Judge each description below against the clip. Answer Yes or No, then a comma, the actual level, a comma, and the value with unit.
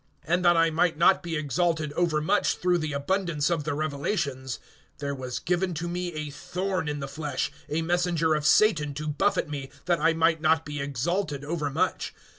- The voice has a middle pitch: Yes, medium, 160 Hz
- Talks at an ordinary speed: Yes, average, 185 wpm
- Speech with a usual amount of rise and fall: Yes, average, 3.0 semitones